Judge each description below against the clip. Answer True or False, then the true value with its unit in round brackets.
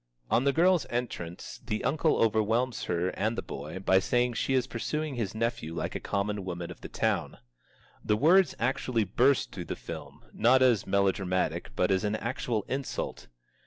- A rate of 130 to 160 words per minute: False (180 wpm)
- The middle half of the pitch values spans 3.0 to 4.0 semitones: False (4.9 semitones)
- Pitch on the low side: True (115 Hz)